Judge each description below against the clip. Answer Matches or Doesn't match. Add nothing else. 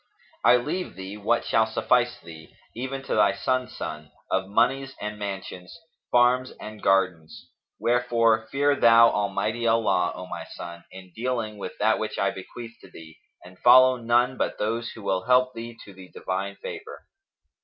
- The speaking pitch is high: Doesn't match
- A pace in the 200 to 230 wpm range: Doesn't match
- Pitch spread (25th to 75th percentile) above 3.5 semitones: Matches